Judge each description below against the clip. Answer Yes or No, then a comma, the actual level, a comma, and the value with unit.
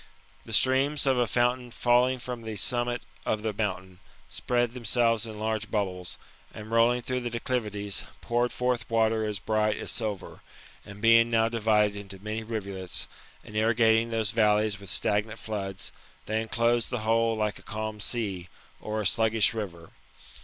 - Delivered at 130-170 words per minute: Yes, average, 160 wpm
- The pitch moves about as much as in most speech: No, narrow, 2.0 semitones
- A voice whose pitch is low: Yes, low, 110 Hz